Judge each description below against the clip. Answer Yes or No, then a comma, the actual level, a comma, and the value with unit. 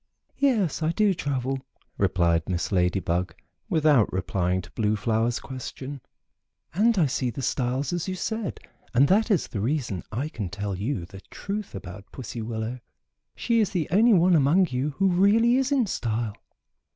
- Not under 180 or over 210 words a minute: No, average, 170 wpm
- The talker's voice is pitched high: No, low, 135 Hz